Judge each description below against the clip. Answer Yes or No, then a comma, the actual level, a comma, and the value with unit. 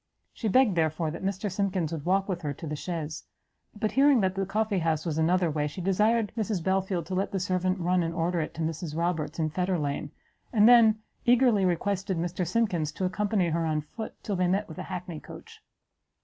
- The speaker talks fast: Yes, fast, 210 wpm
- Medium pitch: Yes, medium, 180 Hz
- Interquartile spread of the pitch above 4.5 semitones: No, average, 3.5 semitones